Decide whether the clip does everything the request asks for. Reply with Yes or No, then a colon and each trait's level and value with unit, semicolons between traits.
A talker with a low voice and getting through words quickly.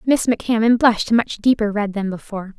No: high, 220 Hz; fast, 210 wpm